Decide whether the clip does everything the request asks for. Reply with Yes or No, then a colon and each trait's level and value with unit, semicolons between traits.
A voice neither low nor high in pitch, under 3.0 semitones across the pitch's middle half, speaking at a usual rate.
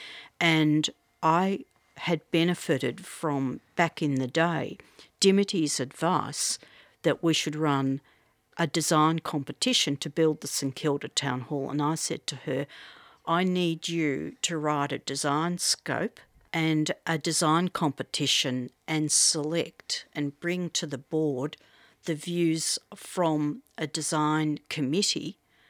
No: medium, 155 Hz; narrow, 2.4 semitones; slow, 130 wpm